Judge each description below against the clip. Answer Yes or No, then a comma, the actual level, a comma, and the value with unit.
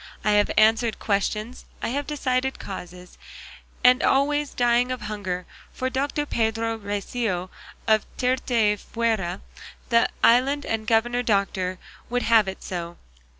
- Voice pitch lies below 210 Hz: No, high, 225 Hz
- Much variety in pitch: No, average, 3.7 semitones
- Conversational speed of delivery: No, slow, 125 wpm